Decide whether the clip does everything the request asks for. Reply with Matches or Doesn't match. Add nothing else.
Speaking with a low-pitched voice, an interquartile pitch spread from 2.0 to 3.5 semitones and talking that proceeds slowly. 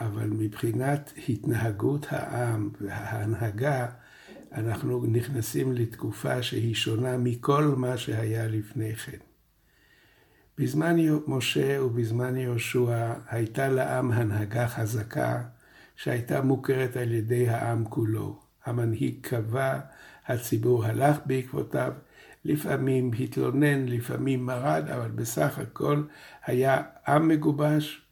Matches